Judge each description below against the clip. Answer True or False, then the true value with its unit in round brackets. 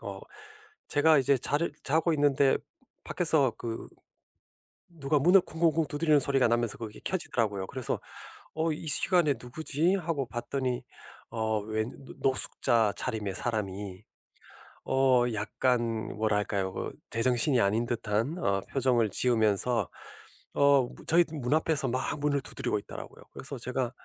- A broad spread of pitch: False (4.8 semitones)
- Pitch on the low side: True (130 Hz)